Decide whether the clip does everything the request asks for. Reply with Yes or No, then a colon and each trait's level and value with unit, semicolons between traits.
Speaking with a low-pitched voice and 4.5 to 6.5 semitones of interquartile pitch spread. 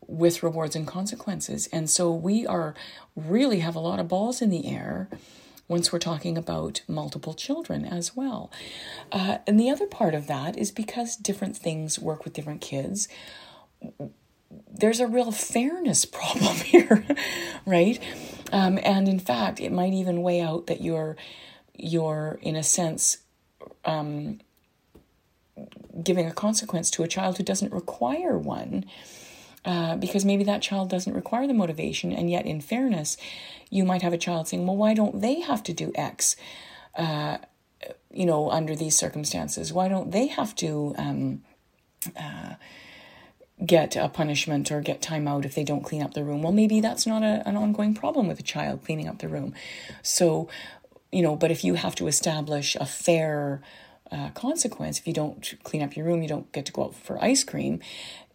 No: medium, 175 Hz; average, 4.9 semitones